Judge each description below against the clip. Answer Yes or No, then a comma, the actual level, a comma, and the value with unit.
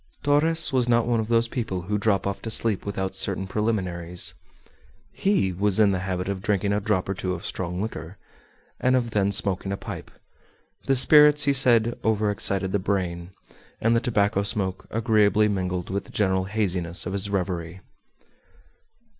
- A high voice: No, low, 100 Hz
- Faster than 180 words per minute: No, average, 170 wpm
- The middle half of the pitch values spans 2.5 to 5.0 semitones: Yes, average, 3.3 semitones